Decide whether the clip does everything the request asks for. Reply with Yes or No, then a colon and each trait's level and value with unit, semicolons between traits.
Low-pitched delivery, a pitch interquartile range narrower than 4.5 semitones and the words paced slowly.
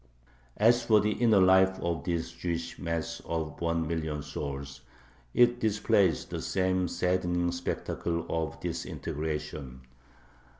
Yes: very low, 85 Hz; average, 3.0 semitones; slow, 120 wpm